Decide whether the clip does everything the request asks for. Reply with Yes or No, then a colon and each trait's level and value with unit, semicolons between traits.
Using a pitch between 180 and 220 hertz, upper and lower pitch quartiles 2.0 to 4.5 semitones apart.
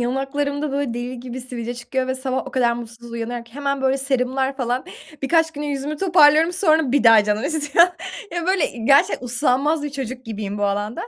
No: very high, 265 Hz; average, 3.3 semitones